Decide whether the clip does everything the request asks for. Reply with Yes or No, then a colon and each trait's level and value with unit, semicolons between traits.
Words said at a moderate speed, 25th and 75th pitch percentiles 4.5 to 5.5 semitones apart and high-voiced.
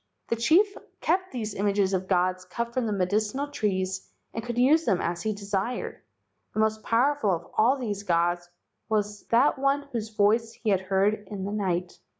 No: average, 180 wpm; average, 3.9 semitones; high, 210 Hz